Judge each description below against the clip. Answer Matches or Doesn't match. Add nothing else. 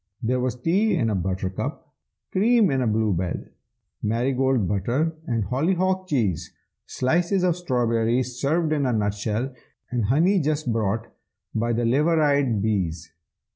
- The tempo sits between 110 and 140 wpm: Matches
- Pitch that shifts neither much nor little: Doesn't match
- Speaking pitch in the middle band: Doesn't match